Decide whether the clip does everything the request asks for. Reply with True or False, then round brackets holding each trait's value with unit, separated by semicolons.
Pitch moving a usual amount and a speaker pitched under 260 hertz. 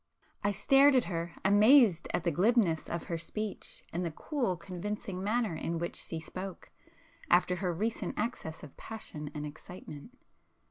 True (4.5 semitones; 185 Hz)